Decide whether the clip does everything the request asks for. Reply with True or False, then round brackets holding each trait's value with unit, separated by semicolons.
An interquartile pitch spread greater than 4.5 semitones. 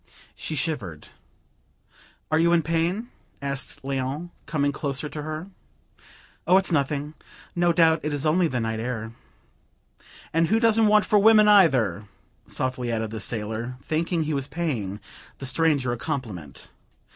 True (5.1 semitones)